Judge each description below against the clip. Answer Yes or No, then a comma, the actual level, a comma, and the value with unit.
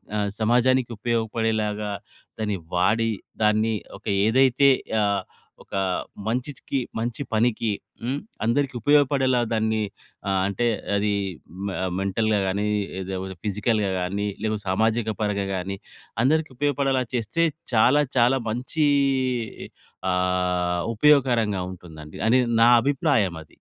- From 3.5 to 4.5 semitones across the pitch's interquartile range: Yes, average, 4.0 semitones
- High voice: No, low, 110 Hz